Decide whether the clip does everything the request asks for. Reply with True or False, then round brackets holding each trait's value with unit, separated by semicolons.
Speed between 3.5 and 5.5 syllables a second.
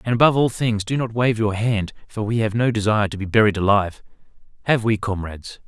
False (6.5 syllables/s)